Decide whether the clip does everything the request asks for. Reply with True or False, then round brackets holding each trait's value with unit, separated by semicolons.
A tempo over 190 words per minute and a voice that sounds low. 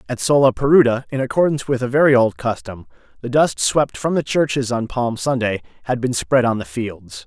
True (200 wpm; 125 Hz)